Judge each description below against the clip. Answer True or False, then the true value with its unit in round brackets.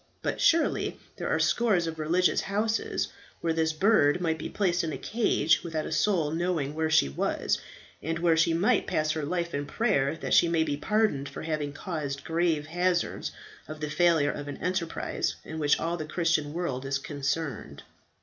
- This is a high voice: False (160 Hz)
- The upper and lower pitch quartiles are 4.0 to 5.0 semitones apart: False (3.0 semitones)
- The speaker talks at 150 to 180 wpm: False (190 wpm)